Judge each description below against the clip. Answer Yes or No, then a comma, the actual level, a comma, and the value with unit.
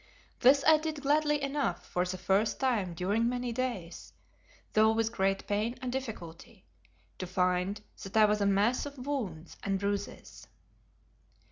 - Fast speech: No, average, 150 wpm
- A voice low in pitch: No, high, 215 Hz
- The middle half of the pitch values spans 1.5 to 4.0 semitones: No, average, 5.1 semitones